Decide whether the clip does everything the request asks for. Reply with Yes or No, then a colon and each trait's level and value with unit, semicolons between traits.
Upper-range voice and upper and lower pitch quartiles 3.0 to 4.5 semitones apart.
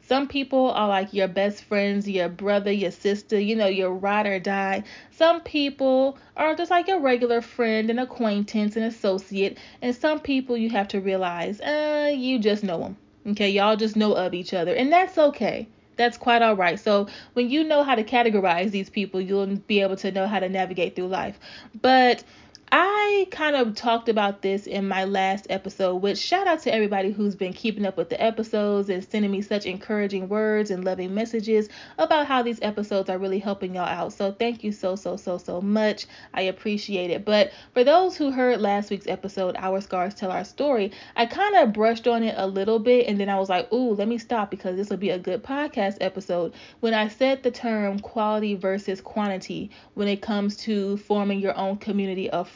Yes: high, 205 Hz; average, 3.6 semitones